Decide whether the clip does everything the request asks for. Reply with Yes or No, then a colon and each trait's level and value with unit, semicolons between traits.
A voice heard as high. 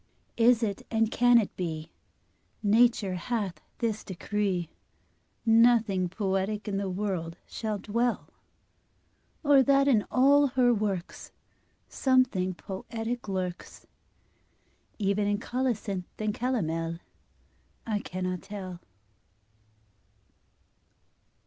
Yes: high, 210 Hz